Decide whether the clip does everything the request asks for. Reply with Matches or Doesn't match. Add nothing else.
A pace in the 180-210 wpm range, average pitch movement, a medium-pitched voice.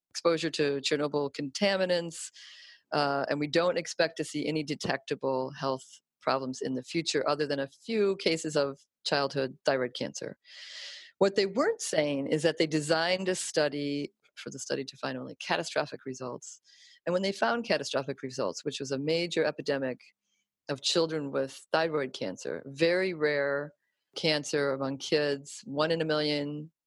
Doesn't match